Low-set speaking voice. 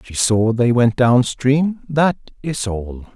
Yes: low, 125 Hz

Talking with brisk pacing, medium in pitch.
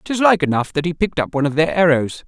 Yes: fast, 290 wpm; medium, 160 Hz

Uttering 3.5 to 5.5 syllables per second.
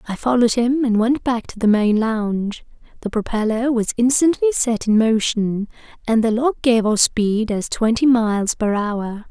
Yes: 4.6 syllables/s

